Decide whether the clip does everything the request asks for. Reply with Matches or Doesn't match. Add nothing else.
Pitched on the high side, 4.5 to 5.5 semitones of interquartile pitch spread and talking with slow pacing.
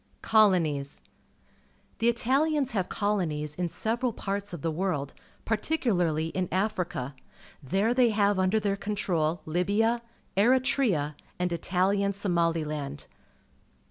Matches